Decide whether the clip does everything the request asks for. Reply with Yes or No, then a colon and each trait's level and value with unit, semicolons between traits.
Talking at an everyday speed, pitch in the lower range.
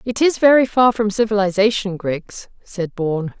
No: average, 160 wpm; high, 210 Hz